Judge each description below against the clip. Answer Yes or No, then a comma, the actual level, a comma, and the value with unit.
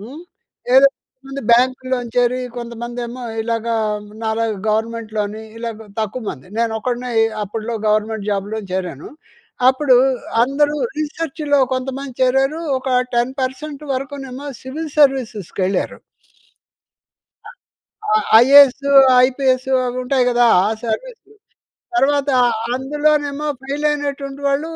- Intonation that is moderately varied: Yes, average, 3.5 semitones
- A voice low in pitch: No, very high, 255 Hz